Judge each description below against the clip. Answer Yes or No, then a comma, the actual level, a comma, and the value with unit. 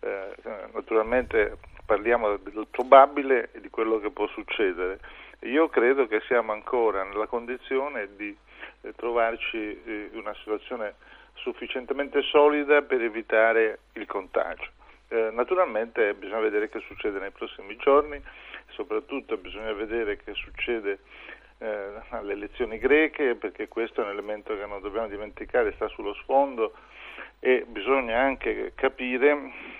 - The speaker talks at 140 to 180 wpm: No, average, 120 wpm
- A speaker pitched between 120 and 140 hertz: Yes, low, 135 Hz